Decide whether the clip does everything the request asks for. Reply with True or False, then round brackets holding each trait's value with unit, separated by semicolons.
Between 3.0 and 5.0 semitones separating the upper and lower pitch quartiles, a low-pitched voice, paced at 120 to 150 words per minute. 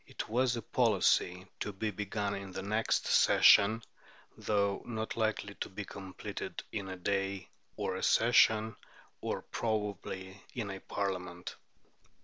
False (2.4 semitones; 100 Hz; 135 wpm)